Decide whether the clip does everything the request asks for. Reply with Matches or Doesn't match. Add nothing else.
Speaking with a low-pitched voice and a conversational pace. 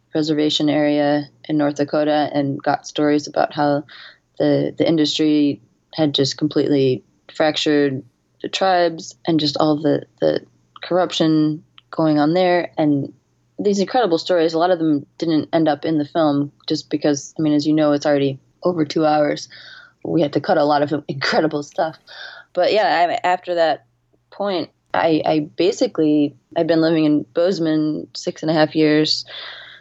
Doesn't match